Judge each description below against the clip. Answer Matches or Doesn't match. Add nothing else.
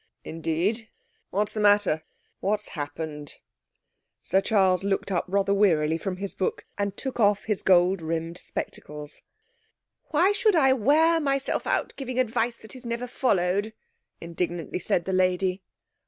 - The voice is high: Matches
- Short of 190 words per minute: Matches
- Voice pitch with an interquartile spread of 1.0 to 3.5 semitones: Doesn't match